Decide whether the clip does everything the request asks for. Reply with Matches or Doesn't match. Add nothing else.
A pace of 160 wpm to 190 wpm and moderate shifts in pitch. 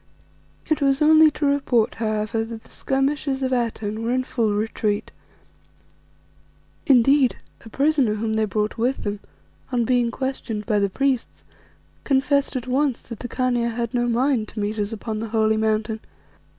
Matches